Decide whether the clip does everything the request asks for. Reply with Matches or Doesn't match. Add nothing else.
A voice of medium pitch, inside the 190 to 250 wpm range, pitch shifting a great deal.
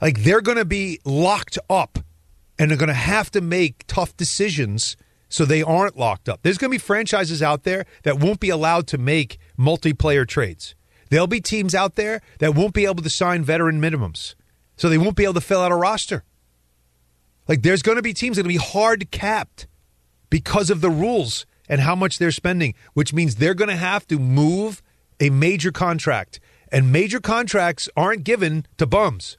Matches